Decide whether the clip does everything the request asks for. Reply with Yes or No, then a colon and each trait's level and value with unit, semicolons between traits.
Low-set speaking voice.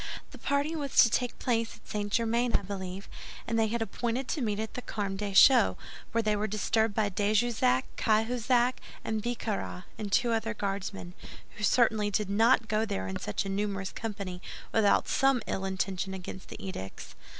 No: high, 215 Hz